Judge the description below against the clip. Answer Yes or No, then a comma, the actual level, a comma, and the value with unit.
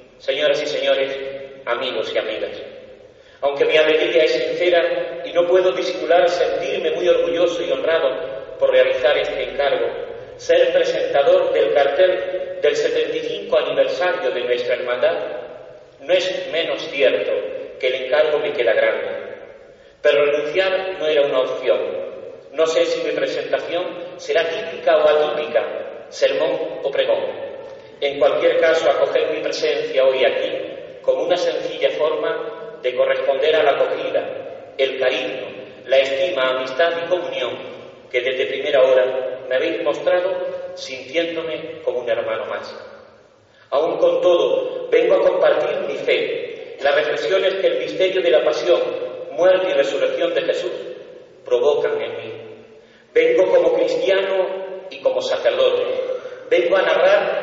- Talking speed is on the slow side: No, average, 135 wpm